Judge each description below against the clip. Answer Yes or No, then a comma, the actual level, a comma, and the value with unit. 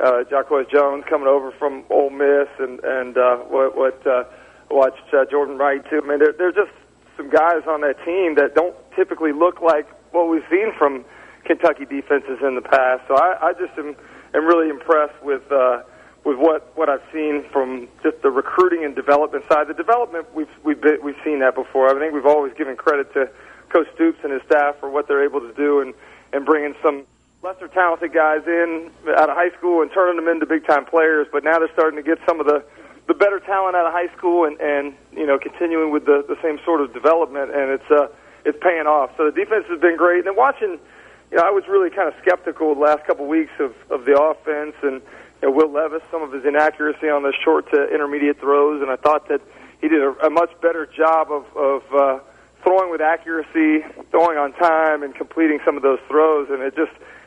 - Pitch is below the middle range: No, medium, 155 Hz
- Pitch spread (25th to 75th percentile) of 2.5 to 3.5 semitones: Yes, average, 3.1 semitones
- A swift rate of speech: Yes, fast, 225 wpm